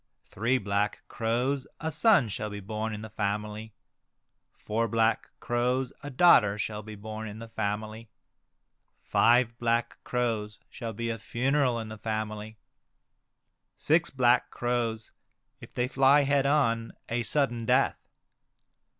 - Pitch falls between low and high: No, low, 115 Hz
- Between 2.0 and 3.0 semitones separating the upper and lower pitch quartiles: Yes, narrow, 2.6 semitones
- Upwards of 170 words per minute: No, slow, 135 wpm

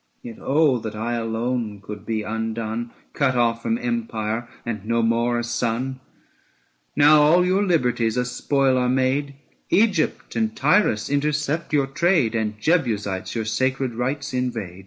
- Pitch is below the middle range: Yes, low, 125 Hz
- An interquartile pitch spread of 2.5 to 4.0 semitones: No, average, 4.5 semitones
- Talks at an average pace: Yes, average, 155 wpm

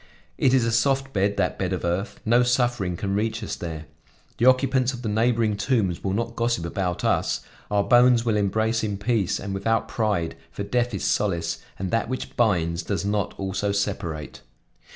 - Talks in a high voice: No, low, 105 Hz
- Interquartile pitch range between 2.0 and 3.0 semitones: No, average, 3.5 semitones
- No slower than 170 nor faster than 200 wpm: Yes, average, 190 wpm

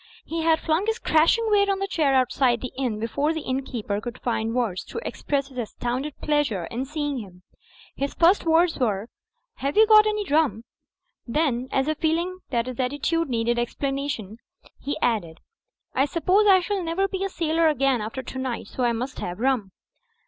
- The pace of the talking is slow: No, average, 190 wpm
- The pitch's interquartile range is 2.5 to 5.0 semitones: No, wide, 5.5 semitones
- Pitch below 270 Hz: No, very high, 275 Hz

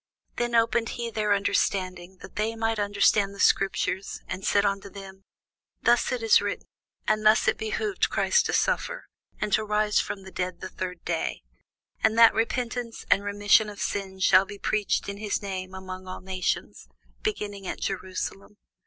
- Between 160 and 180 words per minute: Yes, average, 170 wpm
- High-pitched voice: Yes, high, 205 Hz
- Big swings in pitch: No, narrow, 2.4 semitones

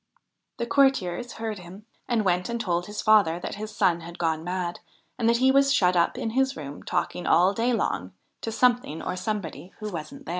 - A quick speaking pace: Yes, fast, 210 wpm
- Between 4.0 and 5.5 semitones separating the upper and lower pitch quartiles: Yes, average, 5.1 semitones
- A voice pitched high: Yes, high, 200 Hz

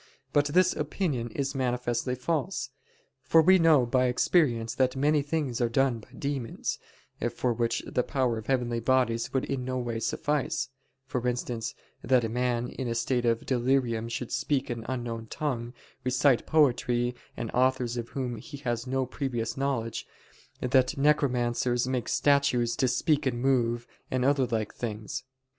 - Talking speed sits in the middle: Yes, average, 160 wpm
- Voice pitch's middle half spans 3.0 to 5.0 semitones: No, narrow, 2.5 semitones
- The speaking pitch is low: Yes, low, 125 Hz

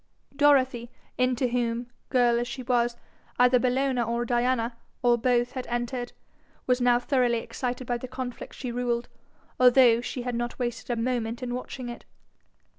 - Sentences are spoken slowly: No, average, 160 wpm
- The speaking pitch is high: Yes, high, 245 Hz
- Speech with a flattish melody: Yes, narrow, 1.0 semitones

